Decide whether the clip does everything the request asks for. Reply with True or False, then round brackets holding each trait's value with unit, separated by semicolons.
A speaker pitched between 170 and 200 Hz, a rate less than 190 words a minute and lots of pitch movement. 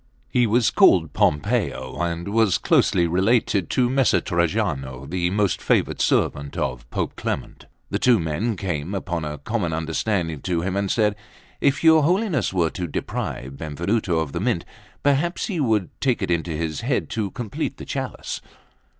False (95 Hz; 165 wpm; 6.1 semitones)